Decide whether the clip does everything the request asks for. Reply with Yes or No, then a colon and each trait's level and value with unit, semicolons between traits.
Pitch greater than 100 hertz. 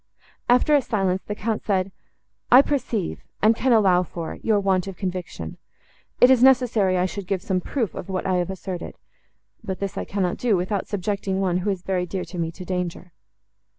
Yes: high, 190 Hz